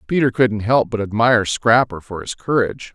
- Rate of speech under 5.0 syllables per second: No, 5.4 syllables/s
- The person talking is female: No, male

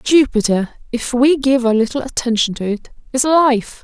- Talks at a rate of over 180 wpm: No, average, 170 wpm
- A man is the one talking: No, female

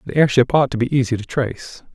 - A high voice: No, low, 130 Hz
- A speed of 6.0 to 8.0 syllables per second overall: Yes, 6.4 syllables/s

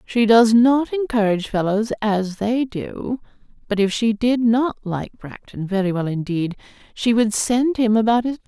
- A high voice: Yes, high, 220 Hz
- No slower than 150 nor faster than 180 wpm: Yes, average, 175 wpm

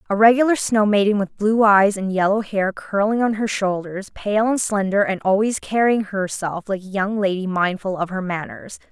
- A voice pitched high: Yes, high, 200 Hz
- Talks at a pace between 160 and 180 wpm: No, average, 195 wpm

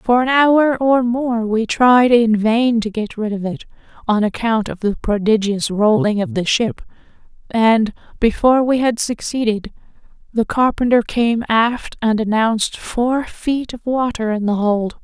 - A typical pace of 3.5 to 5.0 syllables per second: Yes, 4.2 syllables/s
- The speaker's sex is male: No, female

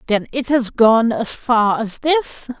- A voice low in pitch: No, high, 235 Hz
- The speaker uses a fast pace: No, average, 185 wpm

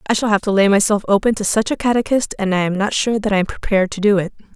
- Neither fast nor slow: No, fast, 305 wpm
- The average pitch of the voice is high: Yes, high, 205 Hz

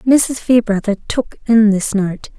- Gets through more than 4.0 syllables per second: No, 3.6 syllables/s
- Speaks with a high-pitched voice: Yes, high, 220 Hz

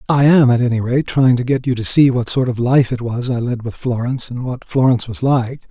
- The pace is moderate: No, fast, 275 wpm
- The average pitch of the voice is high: No, low, 125 Hz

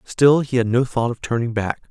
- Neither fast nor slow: No, fast, 250 wpm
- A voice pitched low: Yes, low, 120 Hz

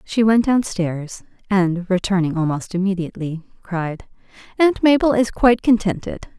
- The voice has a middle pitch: No, high, 200 Hz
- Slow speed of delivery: Yes, slow, 130 wpm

